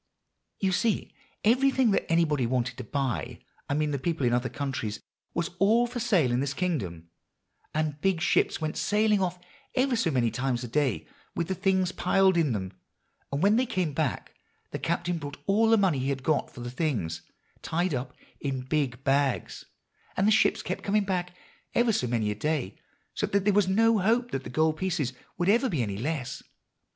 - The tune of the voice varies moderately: No, wide, 6.9 semitones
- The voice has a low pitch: No, medium, 155 Hz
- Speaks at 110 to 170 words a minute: No, average, 195 wpm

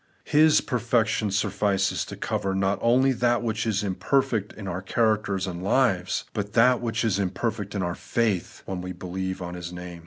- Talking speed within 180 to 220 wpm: Yes, average, 185 wpm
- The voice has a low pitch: Yes, low, 100 Hz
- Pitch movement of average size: Yes, average, 3.7 semitones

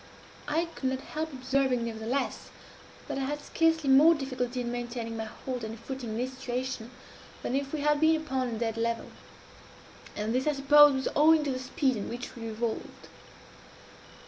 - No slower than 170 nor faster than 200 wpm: Yes, average, 180 wpm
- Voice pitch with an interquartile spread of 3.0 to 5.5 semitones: Yes, average, 3.4 semitones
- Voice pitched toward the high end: Yes, very high, 260 Hz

